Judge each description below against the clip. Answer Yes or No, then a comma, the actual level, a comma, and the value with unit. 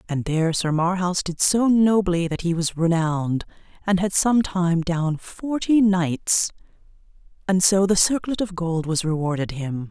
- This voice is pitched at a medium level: Yes, medium, 180 Hz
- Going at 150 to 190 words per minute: Yes, average, 155 wpm